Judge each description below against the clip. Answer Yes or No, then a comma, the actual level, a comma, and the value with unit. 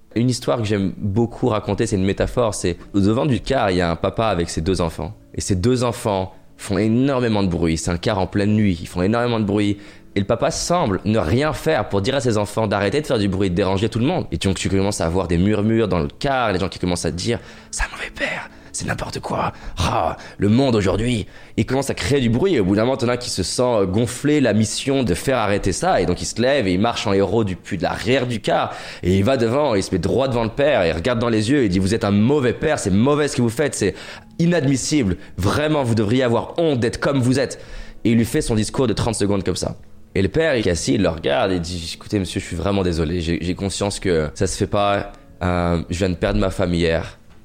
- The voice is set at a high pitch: No, low, 105 Hz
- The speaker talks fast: Yes, fast, 275 wpm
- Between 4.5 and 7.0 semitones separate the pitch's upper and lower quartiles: No, average, 4.1 semitones